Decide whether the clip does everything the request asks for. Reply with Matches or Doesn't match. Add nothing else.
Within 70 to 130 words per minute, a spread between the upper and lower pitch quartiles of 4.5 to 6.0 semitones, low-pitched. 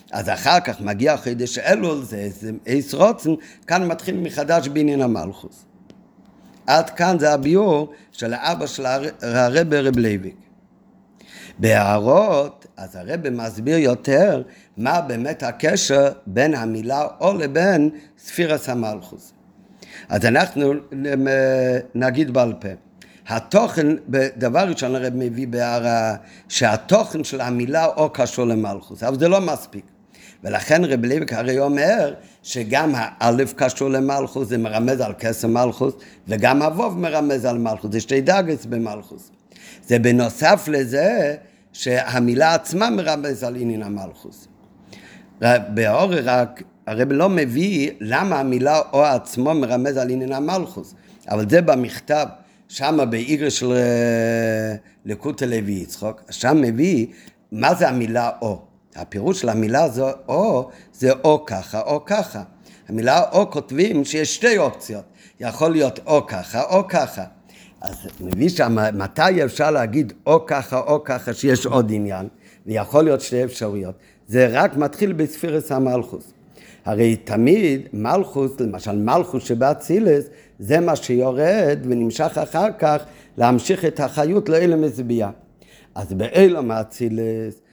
Matches